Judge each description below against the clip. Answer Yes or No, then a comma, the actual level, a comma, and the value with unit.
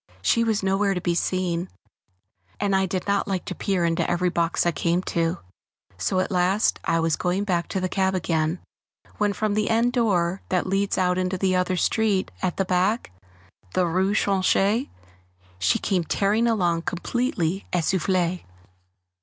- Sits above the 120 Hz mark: Yes, medium, 185 Hz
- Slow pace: No, average, 170 wpm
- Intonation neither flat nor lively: No, narrow, 2.3 semitones